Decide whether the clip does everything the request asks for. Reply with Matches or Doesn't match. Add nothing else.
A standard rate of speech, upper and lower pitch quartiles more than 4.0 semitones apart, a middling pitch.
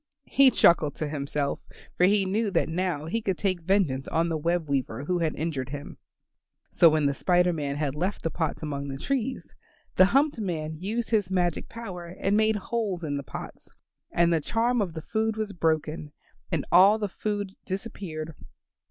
Matches